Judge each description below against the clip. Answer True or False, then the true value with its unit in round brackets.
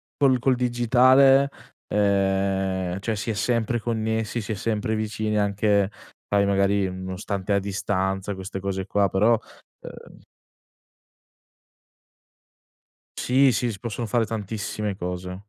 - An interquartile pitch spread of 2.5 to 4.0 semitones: True (2.9 semitones)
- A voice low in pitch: True (105 Hz)